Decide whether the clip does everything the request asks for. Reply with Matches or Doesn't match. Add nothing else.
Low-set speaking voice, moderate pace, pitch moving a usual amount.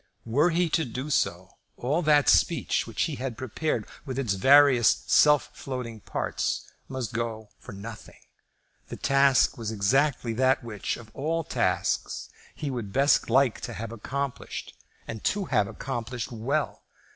Matches